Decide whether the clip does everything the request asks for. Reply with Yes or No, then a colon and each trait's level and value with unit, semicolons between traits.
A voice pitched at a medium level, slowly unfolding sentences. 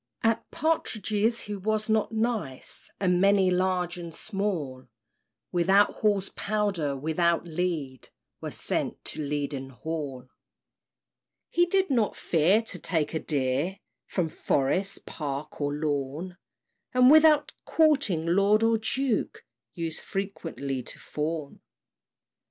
Yes: medium, 180 Hz; slow, 115 wpm